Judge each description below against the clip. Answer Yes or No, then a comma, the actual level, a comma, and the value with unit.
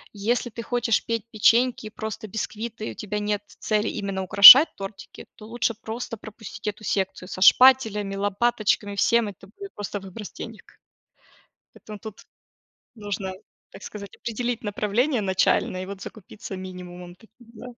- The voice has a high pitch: Yes, high, 210 Hz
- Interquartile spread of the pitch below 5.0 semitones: Yes, narrow, 2.6 semitones